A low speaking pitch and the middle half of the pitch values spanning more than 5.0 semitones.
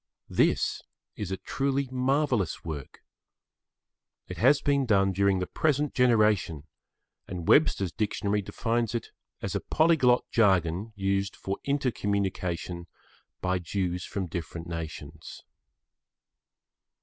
Yes: low, 100 Hz; wide, 5.6 semitones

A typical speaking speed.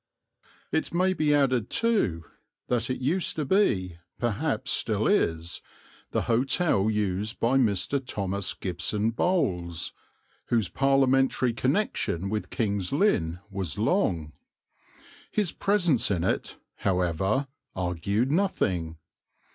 No: slow, 110 wpm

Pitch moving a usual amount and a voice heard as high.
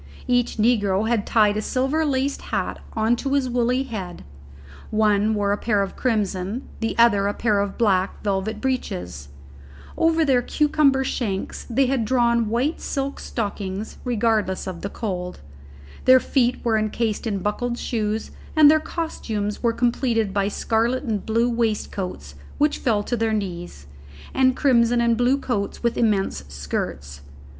Yes: average, 3.6 semitones; high, 225 Hz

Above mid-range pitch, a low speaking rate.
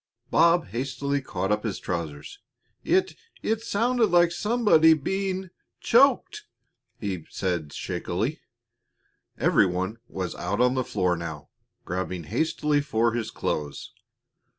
No: low, 130 Hz; slow, 120 wpm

